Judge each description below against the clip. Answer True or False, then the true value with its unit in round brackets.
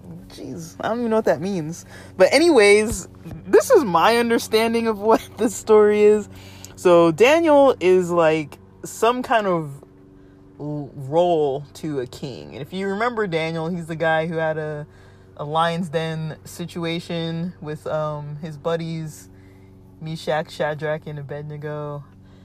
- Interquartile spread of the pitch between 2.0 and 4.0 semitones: False (4.7 semitones)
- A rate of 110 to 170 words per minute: True (140 wpm)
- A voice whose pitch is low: False (160 Hz)